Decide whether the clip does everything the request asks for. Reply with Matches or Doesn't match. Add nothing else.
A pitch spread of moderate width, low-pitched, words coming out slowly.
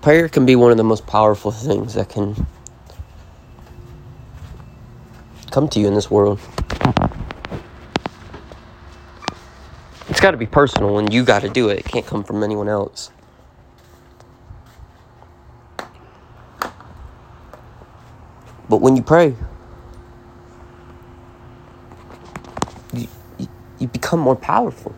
Matches